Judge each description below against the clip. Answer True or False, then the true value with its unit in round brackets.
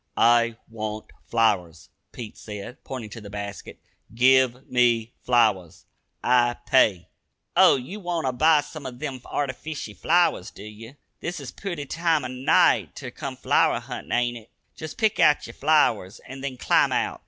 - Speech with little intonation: False (4.5 semitones)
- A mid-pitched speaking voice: False (125 Hz)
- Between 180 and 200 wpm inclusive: False (165 wpm)